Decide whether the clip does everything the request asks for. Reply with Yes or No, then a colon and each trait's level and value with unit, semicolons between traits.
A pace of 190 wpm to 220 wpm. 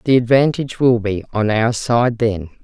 No: average, 180 wpm